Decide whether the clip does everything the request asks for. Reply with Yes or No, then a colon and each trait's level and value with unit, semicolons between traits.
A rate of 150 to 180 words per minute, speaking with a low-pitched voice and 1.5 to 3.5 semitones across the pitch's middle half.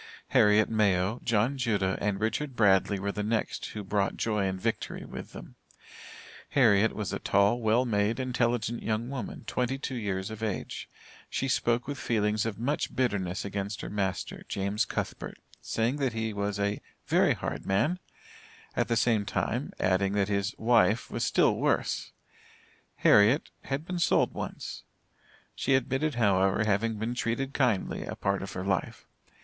Yes: average, 160 wpm; low, 110 Hz; average, 3.2 semitones